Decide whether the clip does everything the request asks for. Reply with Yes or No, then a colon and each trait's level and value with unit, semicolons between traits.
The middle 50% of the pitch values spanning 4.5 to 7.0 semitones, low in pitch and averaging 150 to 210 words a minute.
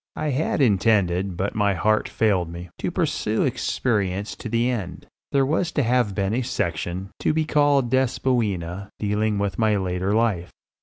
Yes: average, 4.8 semitones; low, 105 Hz; average, 165 wpm